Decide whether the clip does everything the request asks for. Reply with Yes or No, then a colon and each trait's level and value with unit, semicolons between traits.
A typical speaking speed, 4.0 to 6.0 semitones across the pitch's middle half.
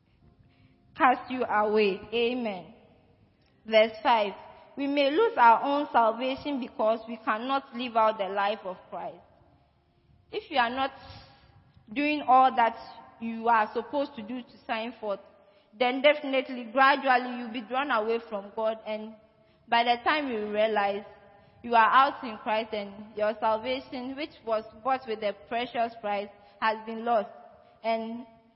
No: average, 145 wpm; average, 3.2 semitones